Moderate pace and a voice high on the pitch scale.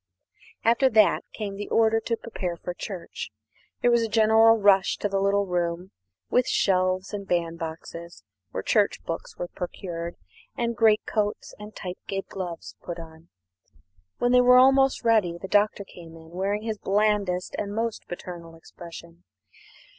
Yes: average, 160 wpm; high, 195 Hz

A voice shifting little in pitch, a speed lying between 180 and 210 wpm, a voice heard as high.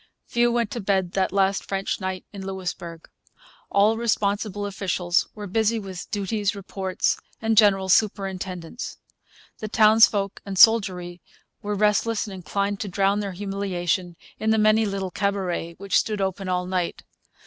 No: narrow, 2.0 semitones; average, 150 wpm; high, 195 Hz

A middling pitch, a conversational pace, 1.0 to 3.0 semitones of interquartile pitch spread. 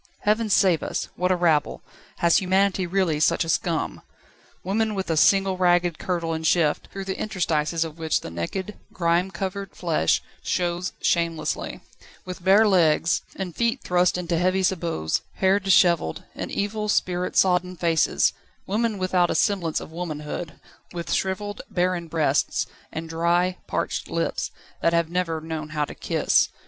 Yes: medium, 180 Hz; average, 155 wpm; narrow, 2.6 semitones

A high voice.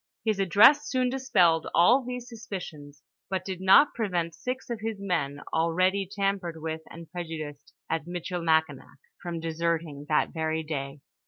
No: medium, 175 Hz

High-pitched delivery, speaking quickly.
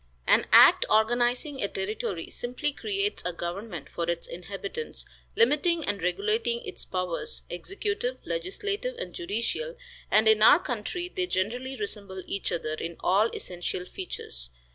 No: high, 235 Hz; average, 140 wpm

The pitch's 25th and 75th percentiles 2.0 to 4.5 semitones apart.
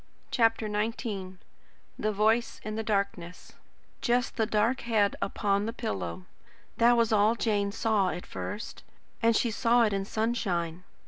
Yes: narrow, 2.5 semitones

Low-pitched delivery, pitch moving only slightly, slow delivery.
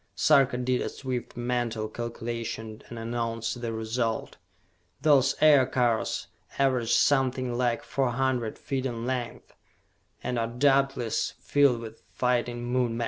Yes: low, 120 Hz; narrow, 2.0 semitones; slow, 130 wpm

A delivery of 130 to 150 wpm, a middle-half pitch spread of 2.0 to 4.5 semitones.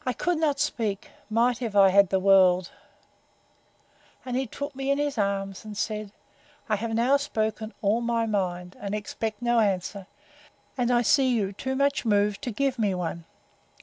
No: average, 180 wpm; average, 4.0 semitones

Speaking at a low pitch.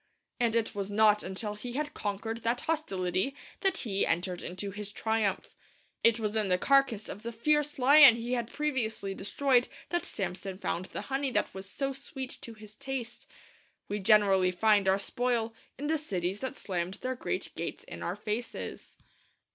No: high, 220 Hz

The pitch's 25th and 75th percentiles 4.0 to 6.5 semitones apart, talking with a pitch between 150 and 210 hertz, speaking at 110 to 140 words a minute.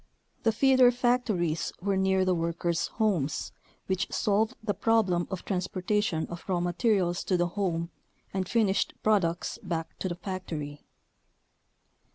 No: average, 3.5 semitones; medium, 185 Hz; slow, 135 wpm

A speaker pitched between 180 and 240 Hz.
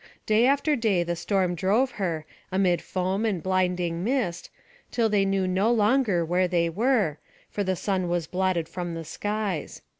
Yes: medium, 185 Hz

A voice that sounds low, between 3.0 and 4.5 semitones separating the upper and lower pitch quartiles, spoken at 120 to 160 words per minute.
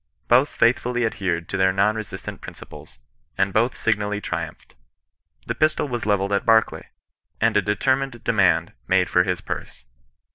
Yes: low, 105 Hz; average, 3.9 semitones; average, 155 wpm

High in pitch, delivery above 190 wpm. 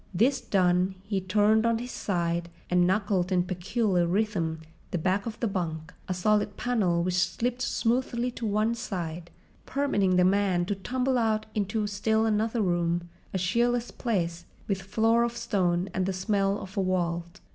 No: high, 195 Hz; average, 170 wpm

